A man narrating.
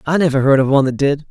Yes: male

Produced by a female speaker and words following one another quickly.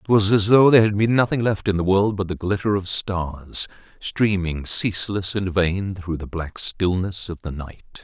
No: male; fast, 210 wpm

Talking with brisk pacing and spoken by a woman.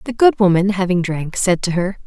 Yes: fast, 235 wpm; female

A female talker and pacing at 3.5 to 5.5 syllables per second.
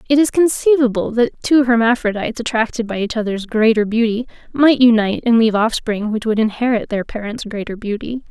No: female; 5.8 syllables/s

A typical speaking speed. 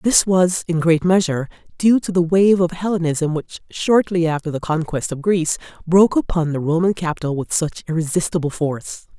Yes: average, 175 wpm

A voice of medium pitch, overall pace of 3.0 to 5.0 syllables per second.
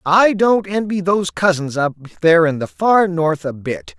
Yes: medium, 170 Hz; 4.7 syllables/s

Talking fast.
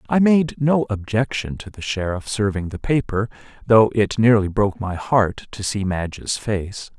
No: average, 170 wpm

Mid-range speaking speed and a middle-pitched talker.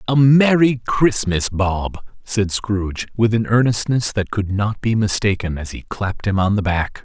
No: average, 180 wpm; low, 105 Hz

